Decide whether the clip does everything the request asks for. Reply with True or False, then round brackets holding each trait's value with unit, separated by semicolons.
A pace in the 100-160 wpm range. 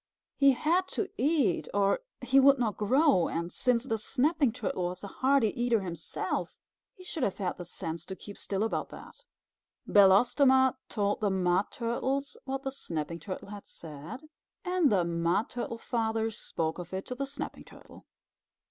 False (170 wpm)